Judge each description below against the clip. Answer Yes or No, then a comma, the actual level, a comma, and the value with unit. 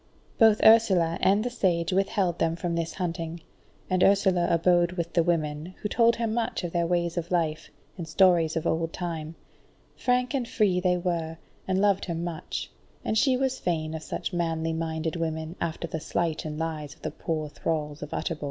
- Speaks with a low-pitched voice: No, medium, 170 Hz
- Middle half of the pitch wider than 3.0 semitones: No, average, 2.7 semitones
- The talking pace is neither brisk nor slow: Yes, average, 190 wpm